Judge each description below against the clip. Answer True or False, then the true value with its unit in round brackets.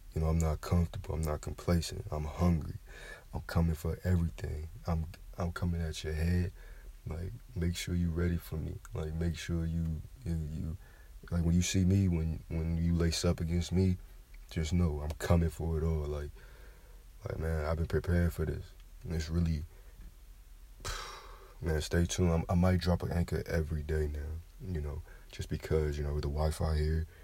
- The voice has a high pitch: False (85 Hz)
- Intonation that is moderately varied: False (2.1 semitones)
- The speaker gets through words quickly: False (185 wpm)